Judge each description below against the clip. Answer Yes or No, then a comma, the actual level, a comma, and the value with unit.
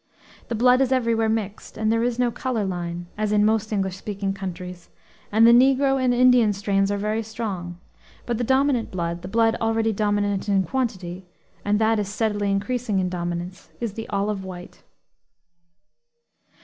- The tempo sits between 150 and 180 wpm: Yes, average, 165 wpm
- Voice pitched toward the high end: Yes, high, 210 Hz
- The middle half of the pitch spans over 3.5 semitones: No, average, 3.1 semitones